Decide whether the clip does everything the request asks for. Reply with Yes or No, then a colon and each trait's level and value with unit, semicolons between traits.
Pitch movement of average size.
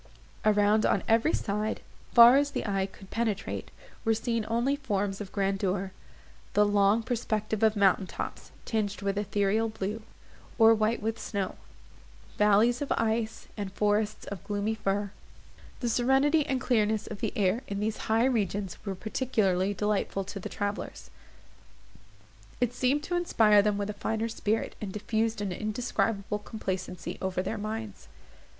No: narrow, 2.1 semitones